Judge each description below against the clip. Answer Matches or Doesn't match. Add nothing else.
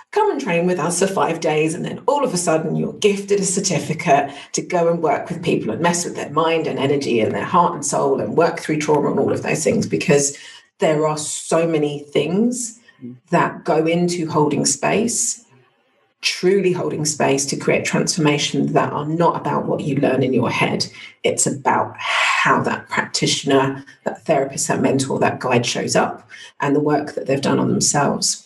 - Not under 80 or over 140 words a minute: Doesn't match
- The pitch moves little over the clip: Doesn't match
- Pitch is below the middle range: Doesn't match